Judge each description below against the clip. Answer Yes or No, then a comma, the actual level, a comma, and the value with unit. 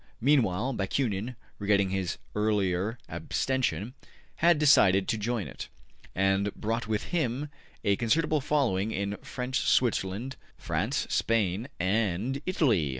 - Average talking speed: No, slow, 120 wpm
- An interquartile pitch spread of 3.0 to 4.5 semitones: No, average, 5.0 semitones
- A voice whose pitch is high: No, low, 110 Hz